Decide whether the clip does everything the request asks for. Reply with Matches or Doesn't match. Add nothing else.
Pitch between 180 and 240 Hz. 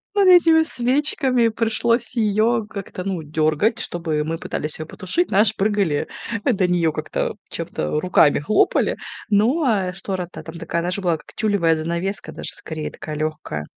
Matches